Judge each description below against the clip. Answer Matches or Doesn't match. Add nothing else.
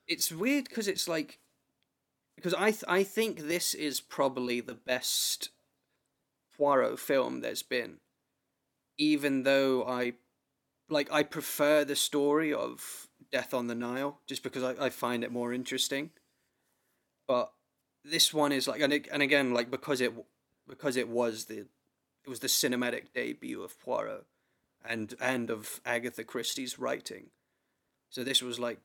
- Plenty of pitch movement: Doesn't match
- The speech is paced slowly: Doesn't match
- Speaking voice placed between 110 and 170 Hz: Matches